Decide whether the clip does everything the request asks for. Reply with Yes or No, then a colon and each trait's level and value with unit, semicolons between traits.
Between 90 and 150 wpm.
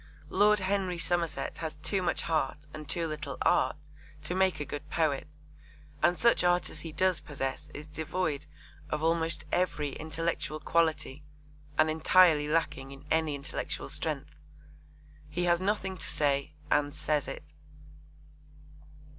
Yes: average, 140 wpm